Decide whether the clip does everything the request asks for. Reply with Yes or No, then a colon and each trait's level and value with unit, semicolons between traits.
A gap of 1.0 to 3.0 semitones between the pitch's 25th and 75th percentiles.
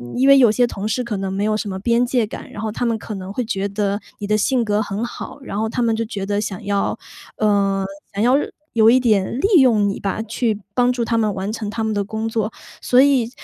Yes: average, 2.7 semitones